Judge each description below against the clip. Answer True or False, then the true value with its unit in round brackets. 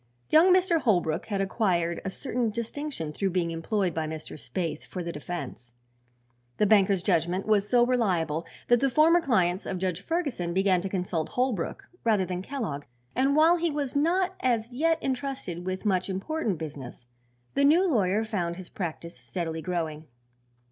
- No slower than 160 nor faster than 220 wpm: True (165 wpm)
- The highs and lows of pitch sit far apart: True (7.0 semitones)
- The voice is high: True (195 Hz)